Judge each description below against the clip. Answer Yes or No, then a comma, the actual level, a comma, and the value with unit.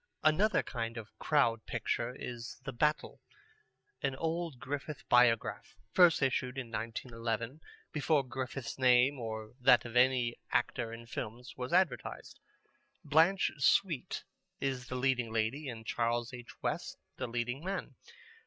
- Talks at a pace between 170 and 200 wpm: No, slow, 135 wpm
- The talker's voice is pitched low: Yes, low, 125 Hz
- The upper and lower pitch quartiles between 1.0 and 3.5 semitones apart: Yes, average, 3.2 semitones